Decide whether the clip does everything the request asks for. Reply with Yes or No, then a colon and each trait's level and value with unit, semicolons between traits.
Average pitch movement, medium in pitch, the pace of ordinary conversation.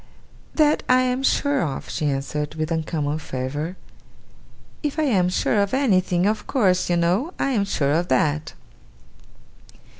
No: wide, 8.7 semitones; medium, 180 Hz; average, 150 wpm